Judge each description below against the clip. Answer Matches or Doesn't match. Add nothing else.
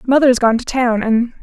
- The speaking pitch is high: Matches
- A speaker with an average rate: Matches